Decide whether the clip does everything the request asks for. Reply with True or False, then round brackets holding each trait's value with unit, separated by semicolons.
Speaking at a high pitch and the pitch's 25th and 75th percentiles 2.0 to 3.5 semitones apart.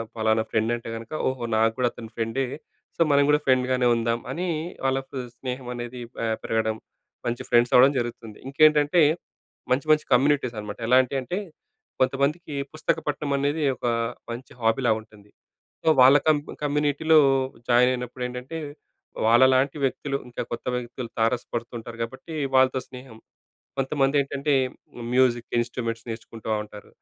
False (125 Hz; 2.9 semitones)